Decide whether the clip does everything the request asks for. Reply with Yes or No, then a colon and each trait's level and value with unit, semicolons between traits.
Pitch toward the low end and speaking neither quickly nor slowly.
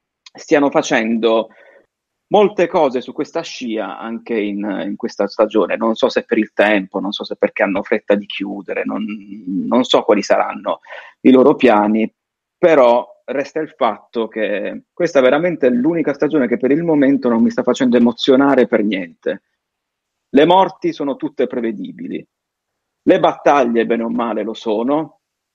Yes: low, 120 Hz; average, 160 wpm